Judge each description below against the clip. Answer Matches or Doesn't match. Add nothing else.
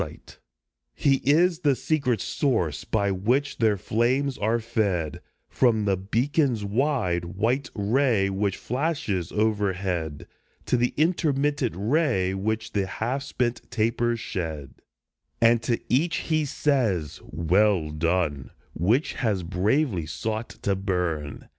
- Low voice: Matches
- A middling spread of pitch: Doesn't match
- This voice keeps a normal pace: Doesn't match